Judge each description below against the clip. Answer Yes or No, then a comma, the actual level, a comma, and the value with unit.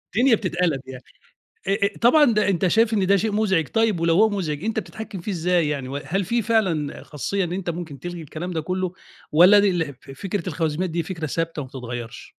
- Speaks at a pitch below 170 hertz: No, medium, 180 Hz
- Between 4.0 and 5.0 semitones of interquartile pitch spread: Yes, average, 4.4 semitones